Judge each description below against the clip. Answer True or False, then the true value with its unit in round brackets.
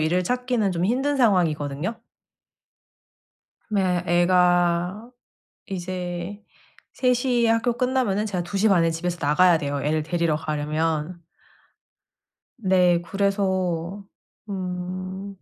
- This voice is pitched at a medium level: True (180 Hz)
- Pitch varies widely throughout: False (3.0 semitones)